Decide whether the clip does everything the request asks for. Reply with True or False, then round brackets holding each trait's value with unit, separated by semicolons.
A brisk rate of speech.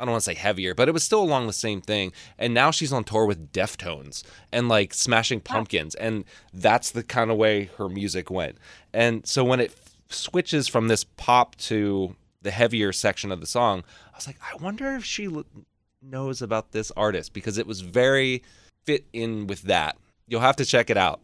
True (210 wpm)